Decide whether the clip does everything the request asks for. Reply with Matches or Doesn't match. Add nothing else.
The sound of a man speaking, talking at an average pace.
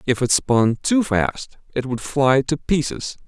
Matches